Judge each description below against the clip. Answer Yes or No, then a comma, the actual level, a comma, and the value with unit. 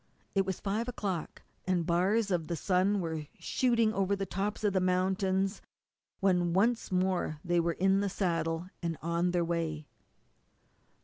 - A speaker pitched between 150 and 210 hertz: Yes, medium, 185 Hz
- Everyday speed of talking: Yes, average, 160 wpm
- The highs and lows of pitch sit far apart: No, narrow, 2.6 semitones